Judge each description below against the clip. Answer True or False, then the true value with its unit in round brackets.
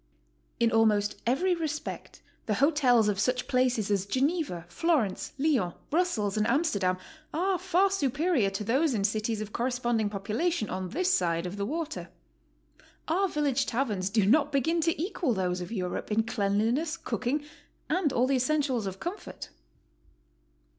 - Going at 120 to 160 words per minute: True (155 wpm)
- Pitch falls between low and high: False (250 Hz)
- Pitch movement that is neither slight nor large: False (7.1 semitones)